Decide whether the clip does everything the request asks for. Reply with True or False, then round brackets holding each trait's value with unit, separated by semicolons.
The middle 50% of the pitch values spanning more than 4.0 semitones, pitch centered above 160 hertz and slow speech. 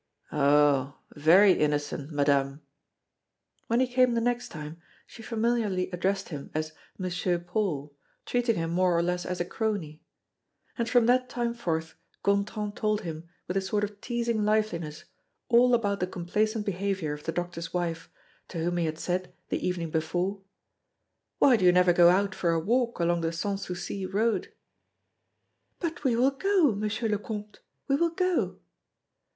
False (5.2 semitones; 185 Hz; 165 wpm)